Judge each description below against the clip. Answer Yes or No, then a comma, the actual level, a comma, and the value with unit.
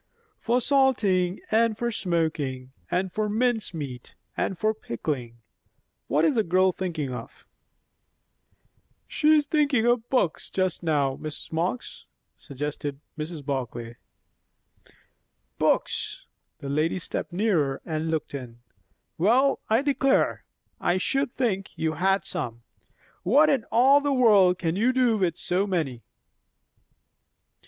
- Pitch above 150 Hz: Yes, medium, 185 Hz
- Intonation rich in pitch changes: Yes, wide, 7.4 semitones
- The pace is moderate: No, slow, 125 wpm